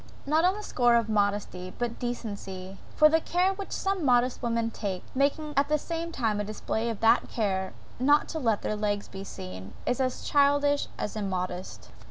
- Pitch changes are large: Yes, wide, 6.0 semitones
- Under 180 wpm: No, average, 190 wpm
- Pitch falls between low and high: No, high, 235 Hz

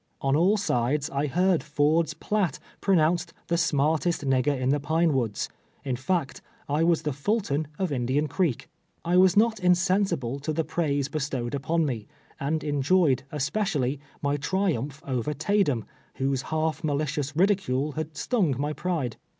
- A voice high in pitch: No, medium, 150 Hz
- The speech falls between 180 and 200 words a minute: No, average, 165 wpm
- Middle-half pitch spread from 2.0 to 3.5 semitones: No, average, 4.0 semitones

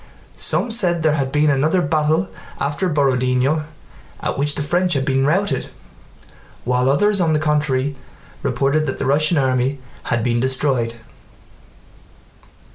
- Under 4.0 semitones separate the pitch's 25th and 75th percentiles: Yes, average, 3.0 semitones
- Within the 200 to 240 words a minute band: No, slow, 135 wpm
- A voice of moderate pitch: Yes, medium, 145 Hz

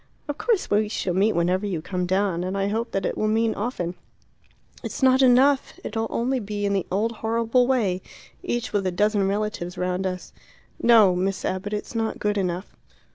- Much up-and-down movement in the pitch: No, average, 3.5 semitones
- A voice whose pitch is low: No, high, 205 Hz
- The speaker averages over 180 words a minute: Yes, average, 190 wpm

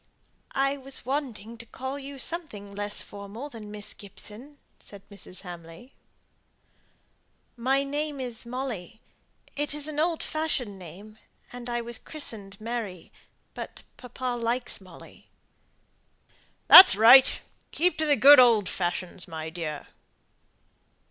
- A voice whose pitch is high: Yes, high, 235 Hz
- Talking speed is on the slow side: Yes, slow, 125 wpm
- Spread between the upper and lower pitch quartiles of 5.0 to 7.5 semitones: Yes, wide, 5.4 semitones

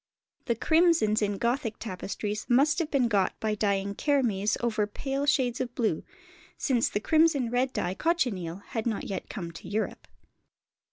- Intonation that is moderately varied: Yes, average, 4.7 semitones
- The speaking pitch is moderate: No, high, 230 Hz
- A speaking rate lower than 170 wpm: Yes, average, 160 wpm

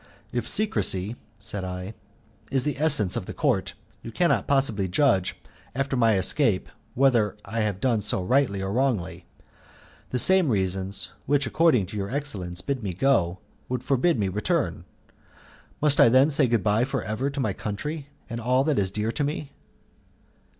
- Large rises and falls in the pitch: Yes, wide, 5.7 semitones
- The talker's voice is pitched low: Yes, low, 115 Hz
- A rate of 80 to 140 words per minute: No, average, 170 wpm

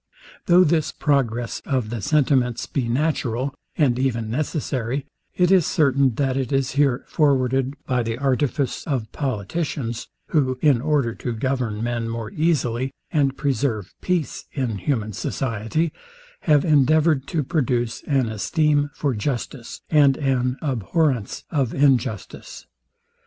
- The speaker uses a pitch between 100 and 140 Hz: Yes, low, 135 Hz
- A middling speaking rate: No, slow, 130 wpm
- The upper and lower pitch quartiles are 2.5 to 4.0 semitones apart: Yes, average, 3.7 semitones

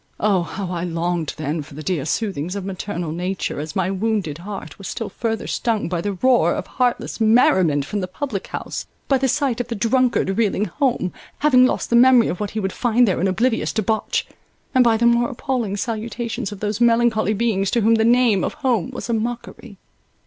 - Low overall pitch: No, high, 215 Hz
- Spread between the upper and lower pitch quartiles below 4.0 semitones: No, average, 4.3 semitones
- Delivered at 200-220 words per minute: Yes, fast, 205 wpm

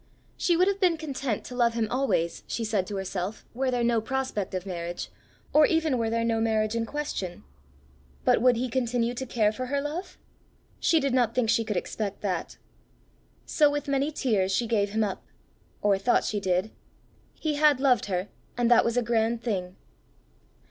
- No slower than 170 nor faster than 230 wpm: Yes, average, 190 wpm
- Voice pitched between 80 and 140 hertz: No, high, 230 Hz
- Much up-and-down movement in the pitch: No, average, 4.3 semitones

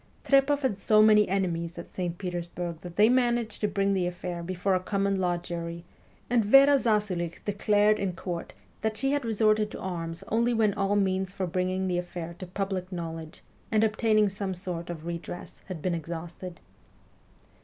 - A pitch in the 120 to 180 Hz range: No, high, 190 Hz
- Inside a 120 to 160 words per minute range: No, average, 175 wpm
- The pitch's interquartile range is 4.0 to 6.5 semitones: No, average, 3.5 semitones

